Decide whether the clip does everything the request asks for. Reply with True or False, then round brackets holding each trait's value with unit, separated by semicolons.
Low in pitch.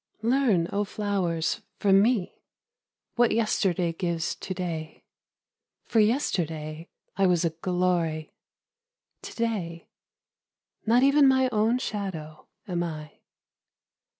False (185 Hz)